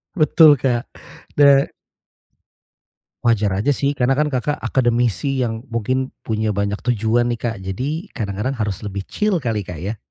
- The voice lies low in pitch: Yes, low, 120 Hz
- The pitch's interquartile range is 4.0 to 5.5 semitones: Yes, average, 4.4 semitones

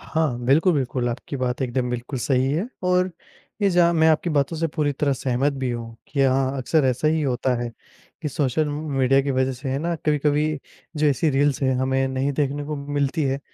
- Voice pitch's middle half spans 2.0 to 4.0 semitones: Yes, narrow, 2.6 semitones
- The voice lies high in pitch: No, medium, 140 Hz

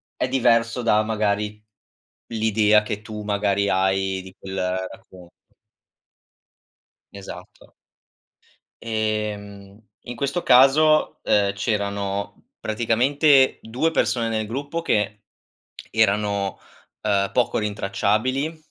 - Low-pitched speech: Yes, low, 105 Hz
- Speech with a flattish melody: No, average, 3.1 semitones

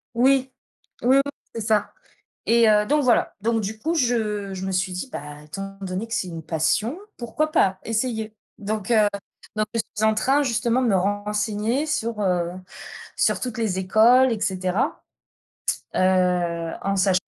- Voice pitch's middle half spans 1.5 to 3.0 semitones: No, average, 3.8 semitones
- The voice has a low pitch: No, high, 215 Hz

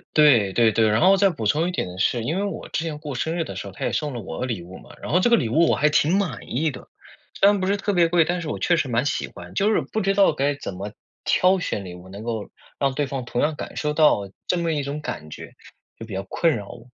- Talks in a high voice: No, medium, 150 Hz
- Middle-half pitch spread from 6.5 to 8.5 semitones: Yes, wide, 7.3 semitones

